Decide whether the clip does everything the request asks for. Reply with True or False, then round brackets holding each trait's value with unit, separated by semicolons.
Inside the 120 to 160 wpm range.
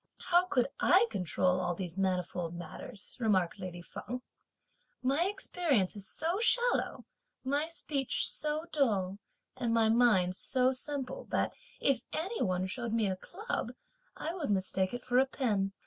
True (150 wpm)